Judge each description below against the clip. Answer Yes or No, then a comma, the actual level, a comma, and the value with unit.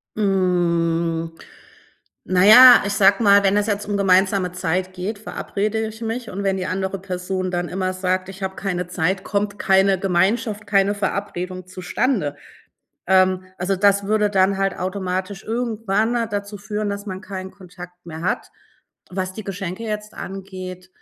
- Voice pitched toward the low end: No, high, 190 Hz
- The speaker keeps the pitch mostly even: Yes, narrow, 1.7 semitones